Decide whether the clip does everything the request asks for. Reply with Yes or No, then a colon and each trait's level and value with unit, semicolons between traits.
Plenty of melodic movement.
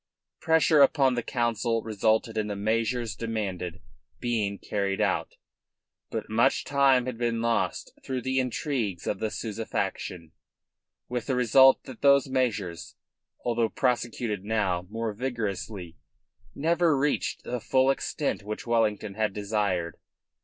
No: average, 3.7 semitones